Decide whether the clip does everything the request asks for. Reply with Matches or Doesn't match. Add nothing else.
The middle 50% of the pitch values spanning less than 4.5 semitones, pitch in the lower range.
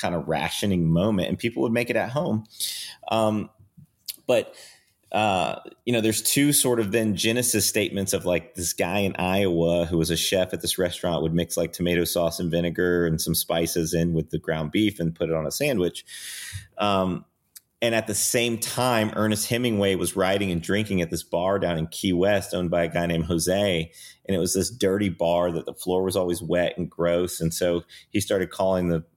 Matches